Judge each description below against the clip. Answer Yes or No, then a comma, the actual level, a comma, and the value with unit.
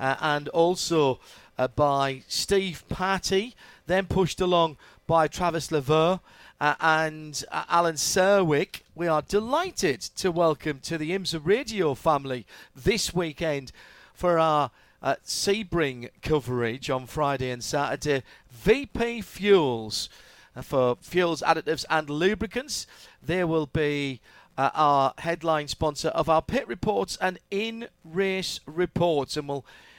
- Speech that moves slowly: Yes, slow, 130 wpm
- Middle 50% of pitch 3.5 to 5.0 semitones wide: Yes, average, 4.5 semitones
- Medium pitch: Yes, medium, 160 Hz